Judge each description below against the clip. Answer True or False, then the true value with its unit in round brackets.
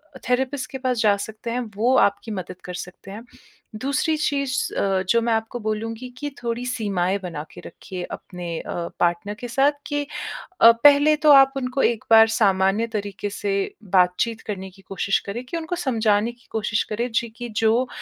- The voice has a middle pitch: False (225 Hz)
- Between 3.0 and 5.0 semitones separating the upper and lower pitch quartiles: True (4.2 semitones)